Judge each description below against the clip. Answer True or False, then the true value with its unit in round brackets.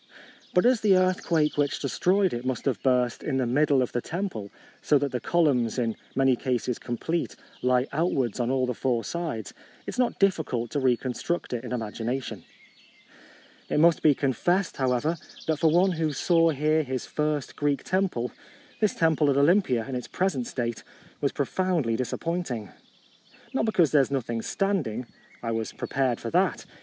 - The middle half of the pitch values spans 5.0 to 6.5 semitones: True (5.4 semitones)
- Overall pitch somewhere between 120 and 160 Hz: True (140 Hz)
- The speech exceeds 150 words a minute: True (175 wpm)